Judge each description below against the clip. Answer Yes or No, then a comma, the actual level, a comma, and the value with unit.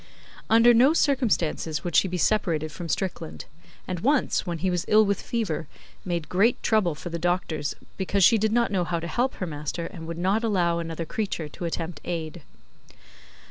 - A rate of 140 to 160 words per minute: No, average, 185 wpm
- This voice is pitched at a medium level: Yes, medium, 180 Hz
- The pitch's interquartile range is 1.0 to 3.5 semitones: No, average, 4.5 semitones